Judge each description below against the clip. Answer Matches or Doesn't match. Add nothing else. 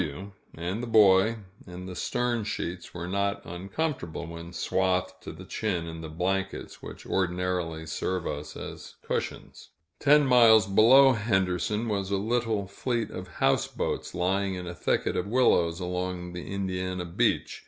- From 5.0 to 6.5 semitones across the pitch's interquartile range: Doesn't match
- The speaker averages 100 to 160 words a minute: Matches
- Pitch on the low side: Matches